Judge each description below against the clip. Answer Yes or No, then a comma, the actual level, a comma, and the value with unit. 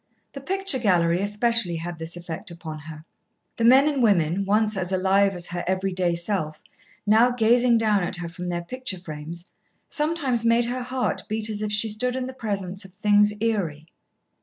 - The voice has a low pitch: No, high, 200 Hz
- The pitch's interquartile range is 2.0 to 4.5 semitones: No, average, 5.0 semitones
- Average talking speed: Yes, average, 185 wpm